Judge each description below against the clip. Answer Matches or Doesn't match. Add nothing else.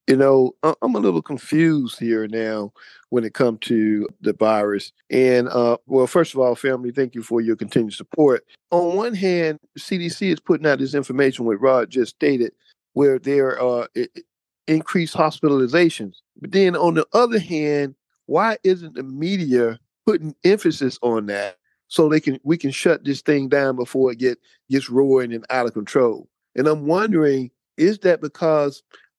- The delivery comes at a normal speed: Matches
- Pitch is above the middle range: Doesn't match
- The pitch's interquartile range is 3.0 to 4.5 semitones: Doesn't match